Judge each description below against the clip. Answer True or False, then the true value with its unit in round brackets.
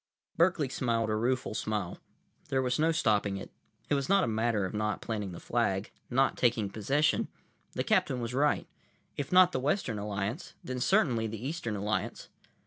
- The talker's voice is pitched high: False (120 Hz)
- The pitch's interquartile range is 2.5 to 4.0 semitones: False (4.5 semitones)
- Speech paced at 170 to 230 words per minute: True (175 wpm)